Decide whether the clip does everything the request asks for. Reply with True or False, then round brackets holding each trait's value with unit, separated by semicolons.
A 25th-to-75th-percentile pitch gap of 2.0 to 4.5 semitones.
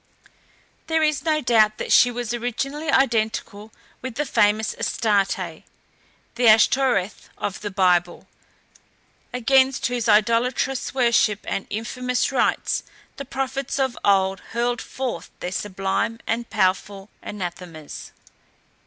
True (4.2 semitones)